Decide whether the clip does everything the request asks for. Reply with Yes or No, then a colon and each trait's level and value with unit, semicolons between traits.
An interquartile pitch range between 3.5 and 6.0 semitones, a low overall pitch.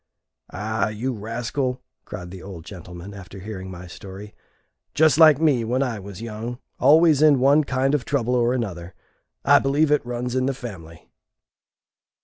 Yes: wide, 5.6 semitones; low, 120 Hz